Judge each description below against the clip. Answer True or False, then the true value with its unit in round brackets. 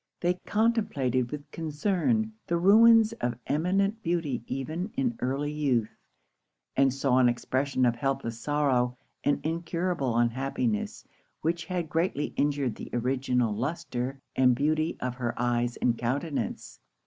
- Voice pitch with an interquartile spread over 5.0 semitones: True (5.4 semitones)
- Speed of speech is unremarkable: False (130 wpm)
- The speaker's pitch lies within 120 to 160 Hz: True (140 Hz)